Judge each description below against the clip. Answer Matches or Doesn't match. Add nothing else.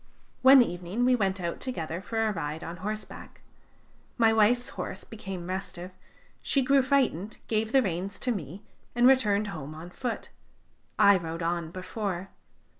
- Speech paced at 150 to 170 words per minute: Matches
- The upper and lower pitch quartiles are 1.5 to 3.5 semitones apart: Doesn't match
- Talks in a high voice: Matches